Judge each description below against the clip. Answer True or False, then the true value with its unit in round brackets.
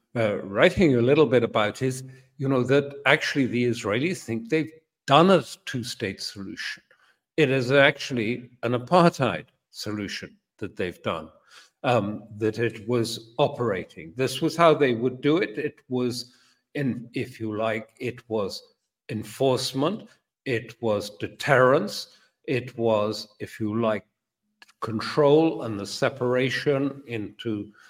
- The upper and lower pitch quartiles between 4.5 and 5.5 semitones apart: False (4.0 semitones)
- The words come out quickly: False (135 wpm)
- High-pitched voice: False (125 Hz)